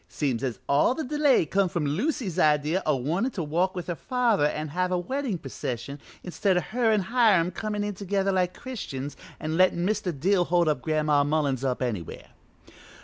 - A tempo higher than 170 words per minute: Yes, average, 185 wpm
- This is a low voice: No, medium, 180 Hz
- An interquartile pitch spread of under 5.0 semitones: No, wide, 5.5 semitones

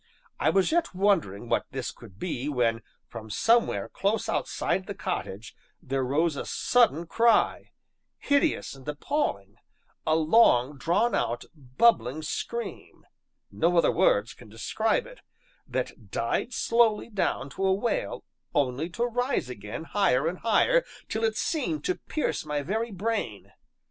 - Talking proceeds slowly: No, average, 145 wpm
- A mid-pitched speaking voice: Yes, medium, 175 Hz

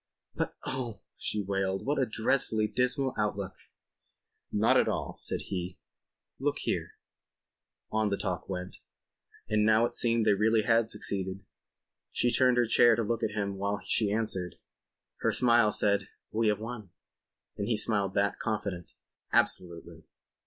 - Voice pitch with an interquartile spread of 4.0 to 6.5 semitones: No, average, 2.8 semitones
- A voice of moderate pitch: No, low, 105 Hz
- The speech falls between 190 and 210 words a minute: No, average, 155 wpm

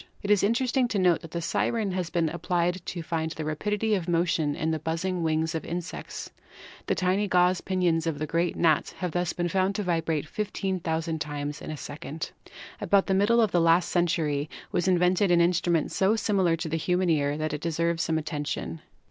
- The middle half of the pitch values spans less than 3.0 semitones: Yes, narrow, 2.6 semitones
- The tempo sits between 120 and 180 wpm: No, average, 200 wpm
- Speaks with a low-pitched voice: No, medium, 170 Hz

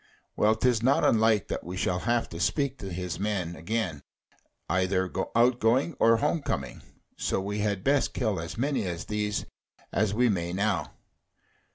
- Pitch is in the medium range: No, low, 105 Hz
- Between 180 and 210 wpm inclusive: No, average, 170 wpm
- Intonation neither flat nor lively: Yes, average, 4.2 semitones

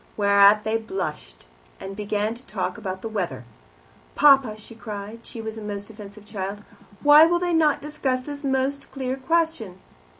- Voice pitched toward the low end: No, high, 220 Hz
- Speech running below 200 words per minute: Yes, average, 165 wpm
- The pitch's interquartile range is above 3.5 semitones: Yes, average, 5.0 semitones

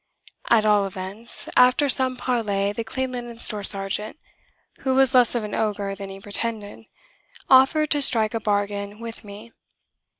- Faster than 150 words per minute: Yes, average, 160 wpm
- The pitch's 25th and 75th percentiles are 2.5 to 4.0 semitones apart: Yes, average, 3.6 semitones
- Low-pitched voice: No, high, 220 Hz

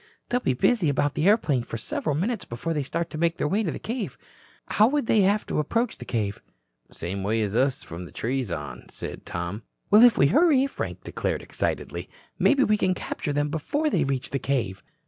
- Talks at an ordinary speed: No, fast, 215 wpm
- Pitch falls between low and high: Yes, medium, 150 Hz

